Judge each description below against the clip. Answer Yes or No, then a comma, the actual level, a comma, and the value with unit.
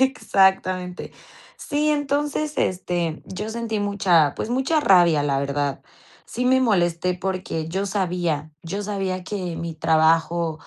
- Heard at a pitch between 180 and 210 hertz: Yes, medium, 185 Hz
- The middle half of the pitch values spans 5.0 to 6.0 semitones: No, average, 4.4 semitones